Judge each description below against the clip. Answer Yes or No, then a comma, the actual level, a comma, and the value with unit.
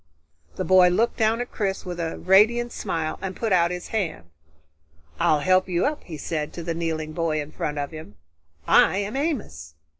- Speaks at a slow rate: No, average, 190 wpm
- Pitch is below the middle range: No, medium, 175 Hz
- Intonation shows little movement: No, average, 4.6 semitones